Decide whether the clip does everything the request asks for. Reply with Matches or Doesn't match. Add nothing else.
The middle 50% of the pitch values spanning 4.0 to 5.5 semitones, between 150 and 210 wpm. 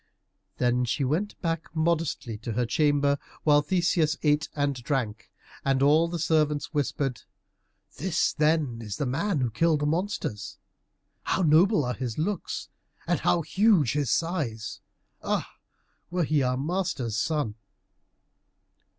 Doesn't match